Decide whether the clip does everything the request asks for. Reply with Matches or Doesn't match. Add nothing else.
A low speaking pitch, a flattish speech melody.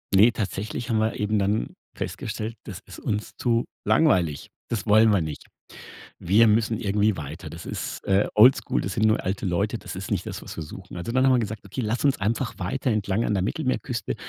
Doesn't match